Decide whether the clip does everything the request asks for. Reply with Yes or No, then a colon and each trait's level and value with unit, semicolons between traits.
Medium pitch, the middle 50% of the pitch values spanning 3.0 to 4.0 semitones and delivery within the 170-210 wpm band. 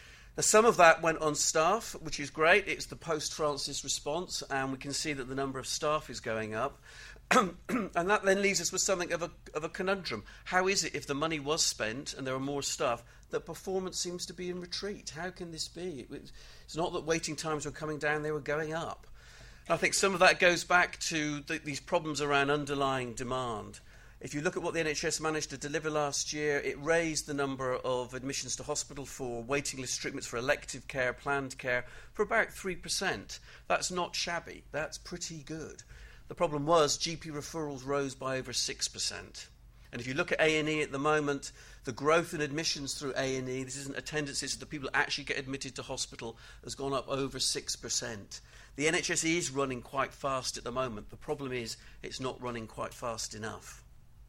Yes: medium, 145 Hz; average, 3.7 semitones; fast, 205 wpm